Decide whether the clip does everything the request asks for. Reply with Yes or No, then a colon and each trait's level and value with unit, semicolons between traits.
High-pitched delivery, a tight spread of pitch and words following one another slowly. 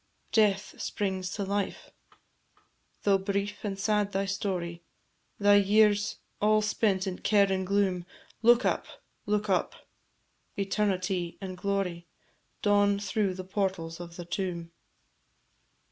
Yes: high, 195 Hz; narrow, 1.8 semitones; slow, 120 wpm